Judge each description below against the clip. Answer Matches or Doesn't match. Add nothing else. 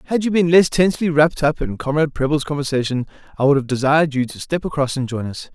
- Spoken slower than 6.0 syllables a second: Doesn't match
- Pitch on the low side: Doesn't match